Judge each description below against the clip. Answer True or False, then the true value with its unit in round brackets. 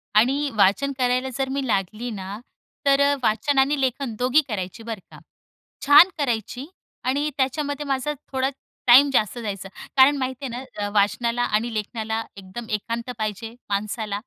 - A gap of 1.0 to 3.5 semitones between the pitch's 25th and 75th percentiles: False (4.2 semitones)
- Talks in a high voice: True (245 Hz)